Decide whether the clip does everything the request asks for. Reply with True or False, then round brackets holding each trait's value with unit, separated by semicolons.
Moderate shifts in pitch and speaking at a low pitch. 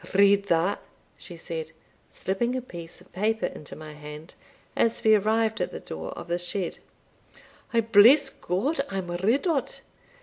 False (4.9 semitones; 200 Hz)